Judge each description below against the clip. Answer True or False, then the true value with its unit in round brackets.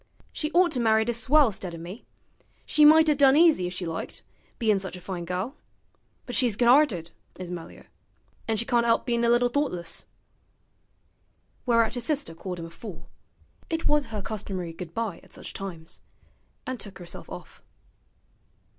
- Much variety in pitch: True (6.1 semitones)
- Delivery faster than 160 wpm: True (175 wpm)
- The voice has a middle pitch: False (225 Hz)